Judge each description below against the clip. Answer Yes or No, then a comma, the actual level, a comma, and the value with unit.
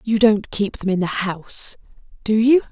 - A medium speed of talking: Yes, average, 175 wpm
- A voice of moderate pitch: No, high, 210 Hz